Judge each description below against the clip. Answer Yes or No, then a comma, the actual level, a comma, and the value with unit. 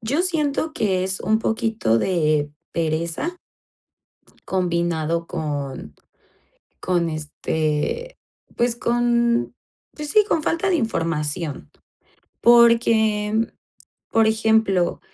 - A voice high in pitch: Yes, high, 210 Hz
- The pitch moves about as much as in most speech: No, wide, 6.4 semitones